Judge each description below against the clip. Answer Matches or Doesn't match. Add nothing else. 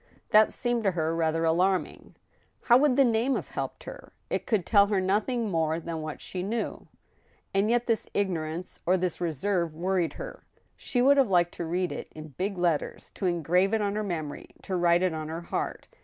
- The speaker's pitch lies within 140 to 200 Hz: Matches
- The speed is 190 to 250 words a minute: Matches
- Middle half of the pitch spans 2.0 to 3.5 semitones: Doesn't match